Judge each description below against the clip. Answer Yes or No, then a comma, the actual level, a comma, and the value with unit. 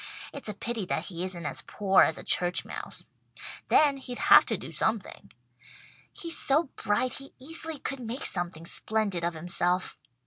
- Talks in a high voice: Yes, high, 210 Hz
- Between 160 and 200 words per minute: Yes, average, 170 wpm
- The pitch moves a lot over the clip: Yes, wide, 7.2 semitones